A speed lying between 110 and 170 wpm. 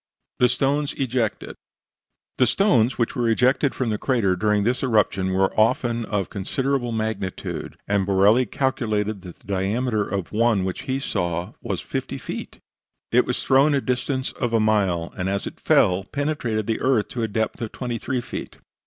No: average, 180 wpm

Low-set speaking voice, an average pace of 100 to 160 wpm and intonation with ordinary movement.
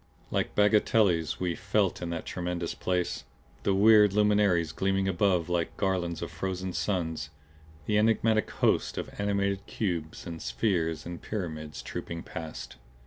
Yes: very low, 90 Hz; average, 140 wpm; average, 3.3 semitones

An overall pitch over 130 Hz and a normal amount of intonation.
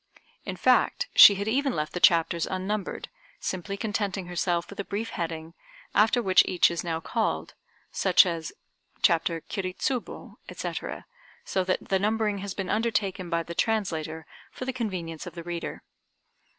Yes: high, 190 Hz; average, 3.8 semitones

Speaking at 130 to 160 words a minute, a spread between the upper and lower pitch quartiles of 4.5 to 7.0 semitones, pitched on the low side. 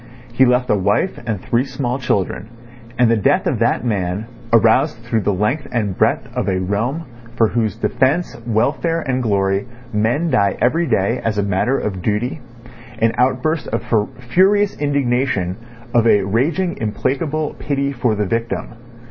Yes: average, 155 wpm; average, 4.8 semitones; low, 120 Hz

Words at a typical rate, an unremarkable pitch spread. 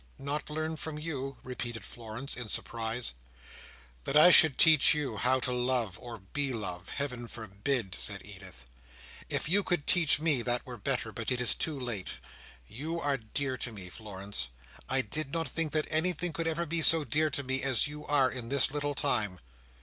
Yes: average, 190 wpm; average, 4.8 semitones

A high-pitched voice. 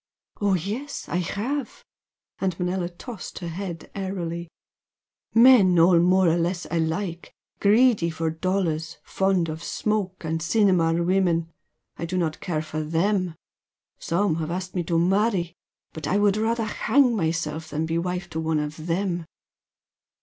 No: medium, 175 Hz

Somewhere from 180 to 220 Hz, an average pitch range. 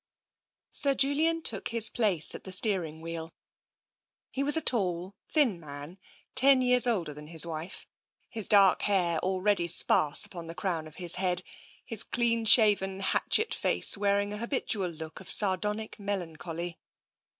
Yes: high, 190 Hz; average, 4.9 semitones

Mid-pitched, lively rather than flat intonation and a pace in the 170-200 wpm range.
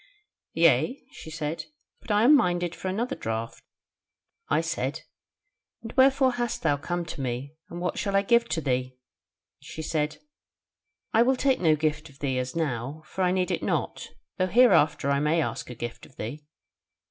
Yes: medium, 165 Hz; wide, 7.4 semitones; average, 180 wpm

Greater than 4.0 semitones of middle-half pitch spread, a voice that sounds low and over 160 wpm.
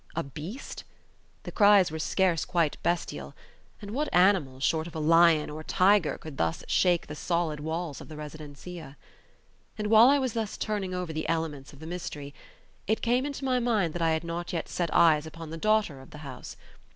No: average, 4.6 semitones; medium, 165 Hz; average, 200 wpm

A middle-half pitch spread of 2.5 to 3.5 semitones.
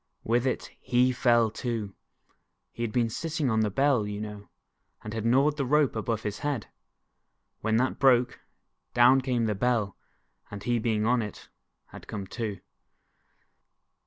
Yes: average, 3.0 semitones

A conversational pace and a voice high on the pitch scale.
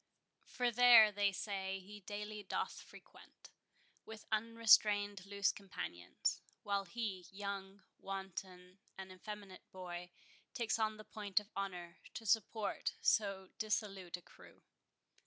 No: slow, 120 wpm; high, 200 Hz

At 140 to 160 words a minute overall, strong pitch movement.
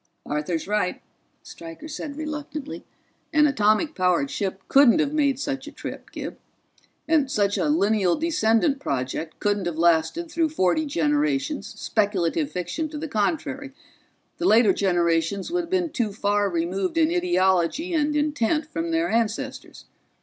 Yes: average, 145 wpm; wide, 8.4 semitones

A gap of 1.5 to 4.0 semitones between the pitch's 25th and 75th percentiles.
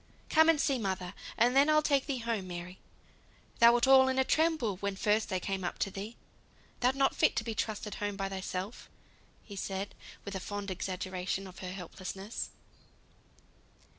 No: average, 4.9 semitones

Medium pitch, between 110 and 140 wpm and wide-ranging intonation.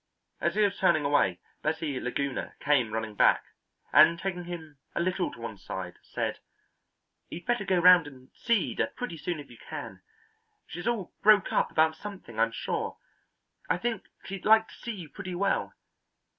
No: medium, 170 Hz; average, 175 wpm; wide, 5.7 semitones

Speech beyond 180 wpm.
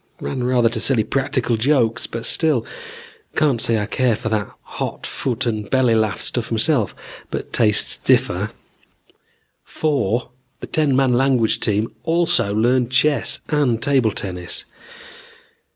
No: slow, 135 wpm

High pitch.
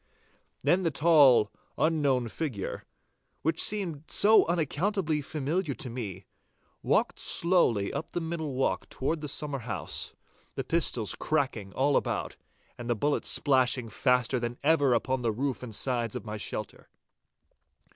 No: low, 135 Hz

